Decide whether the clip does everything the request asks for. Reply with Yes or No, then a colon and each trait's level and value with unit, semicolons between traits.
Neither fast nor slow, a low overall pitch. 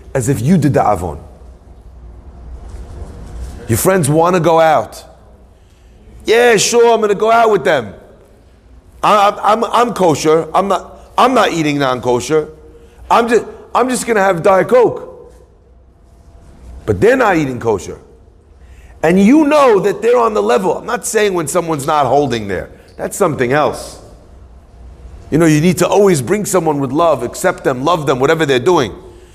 No: average, 170 wpm; medium, 150 Hz